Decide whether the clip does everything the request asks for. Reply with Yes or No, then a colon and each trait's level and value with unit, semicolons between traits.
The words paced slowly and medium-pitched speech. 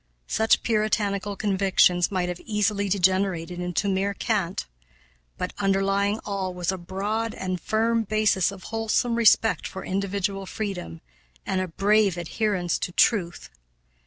No: slow, 130 wpm; high, 195 Hz